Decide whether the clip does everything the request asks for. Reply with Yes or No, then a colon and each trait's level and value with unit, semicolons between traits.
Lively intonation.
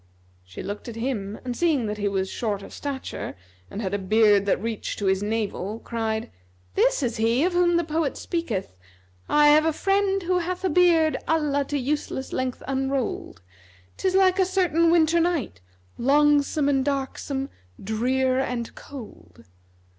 Yes: wide, 6.7 semitones